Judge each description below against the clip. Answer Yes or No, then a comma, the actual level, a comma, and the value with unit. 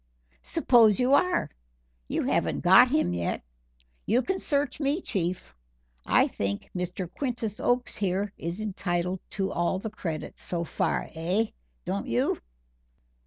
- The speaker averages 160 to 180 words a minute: No, slow, 135 wpm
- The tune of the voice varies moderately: No, wide, 5.9 semitones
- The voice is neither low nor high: No, high, 195 Hz